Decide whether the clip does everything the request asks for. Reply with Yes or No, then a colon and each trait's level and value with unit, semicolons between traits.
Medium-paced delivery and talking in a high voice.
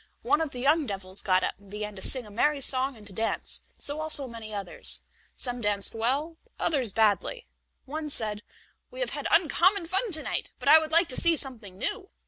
No: fast, 210 wpm; very high, 260 Hz